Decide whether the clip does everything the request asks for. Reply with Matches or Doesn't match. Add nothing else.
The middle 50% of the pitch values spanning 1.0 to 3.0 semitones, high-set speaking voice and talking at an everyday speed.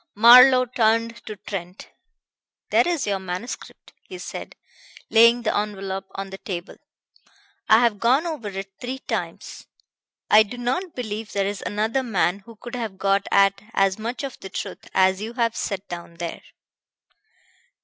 Doesn't match